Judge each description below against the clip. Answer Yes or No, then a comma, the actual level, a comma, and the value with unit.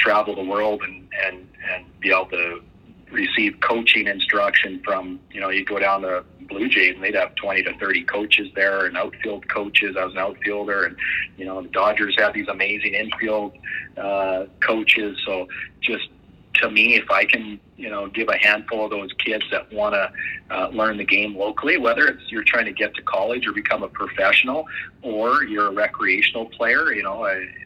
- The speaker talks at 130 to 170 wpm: No, average, 195 wpm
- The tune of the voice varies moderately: No, narrow, 1.8 semitones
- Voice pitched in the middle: No, low, 100 Hz